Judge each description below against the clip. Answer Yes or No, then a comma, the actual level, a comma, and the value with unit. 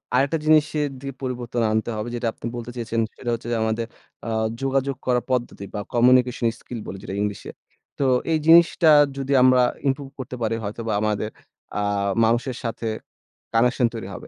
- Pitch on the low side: Yes, low, 120 Hz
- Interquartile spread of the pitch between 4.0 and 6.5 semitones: No, average, 2.8 semitones